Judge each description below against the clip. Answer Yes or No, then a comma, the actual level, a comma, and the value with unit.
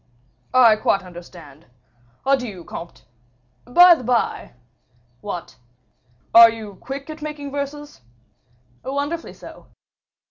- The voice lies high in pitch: Yes, high, 235 Hz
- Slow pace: Yes, slow, 105 wpm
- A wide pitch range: Yes, wide, 8.0 semitones